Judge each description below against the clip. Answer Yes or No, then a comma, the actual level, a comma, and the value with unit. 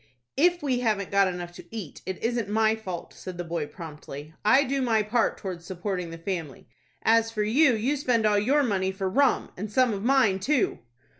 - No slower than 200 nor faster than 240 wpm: Yes, fast, 205 wpm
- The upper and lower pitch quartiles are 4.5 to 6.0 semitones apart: Yes, average, 4.8 semitones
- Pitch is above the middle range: Yes, high, 210 Hz